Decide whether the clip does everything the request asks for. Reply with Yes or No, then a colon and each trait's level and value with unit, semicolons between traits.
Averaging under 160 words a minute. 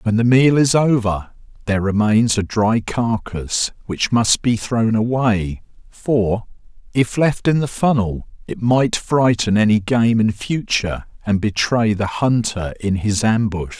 Yes: average, 150 wpm